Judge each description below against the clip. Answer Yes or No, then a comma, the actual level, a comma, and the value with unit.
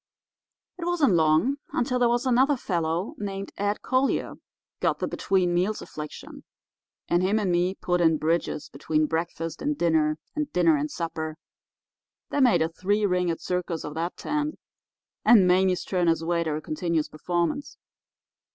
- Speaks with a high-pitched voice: No, medium, 175 Hz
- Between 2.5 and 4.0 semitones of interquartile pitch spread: No, average, 4.5 semitones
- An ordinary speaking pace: Yes, average, 155 wpm